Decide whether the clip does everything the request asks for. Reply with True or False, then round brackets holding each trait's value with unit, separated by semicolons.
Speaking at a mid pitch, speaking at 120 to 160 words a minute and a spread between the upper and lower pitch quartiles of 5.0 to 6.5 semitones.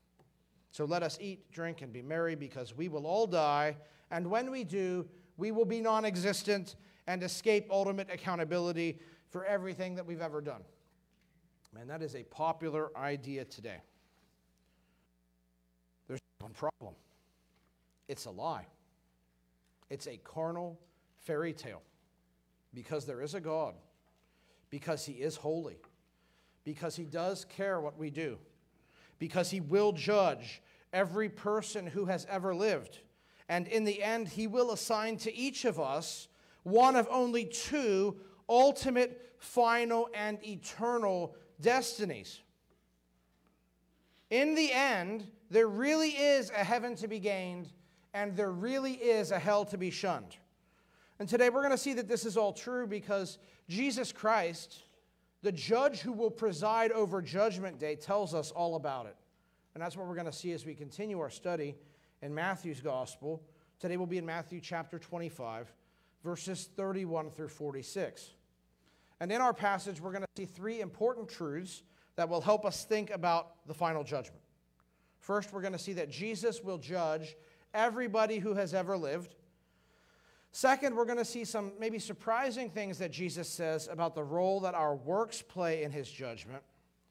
True (180 Hz; 155 wpm; 5.6 semitones)